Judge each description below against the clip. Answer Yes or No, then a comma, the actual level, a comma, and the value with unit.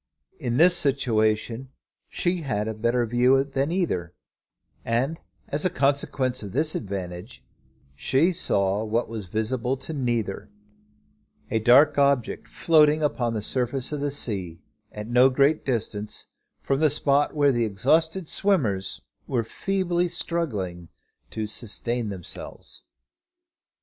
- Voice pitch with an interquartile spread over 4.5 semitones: Yes, average, 5.3 semitones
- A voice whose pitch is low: Yes, low, 125 Hz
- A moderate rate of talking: No, slow, 130 wpm